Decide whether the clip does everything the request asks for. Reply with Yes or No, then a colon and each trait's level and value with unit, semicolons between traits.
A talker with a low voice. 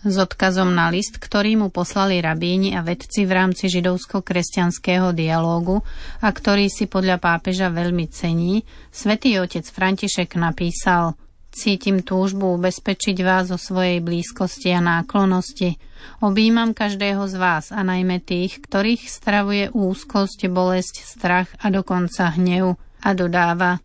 No: medium, 185 Hz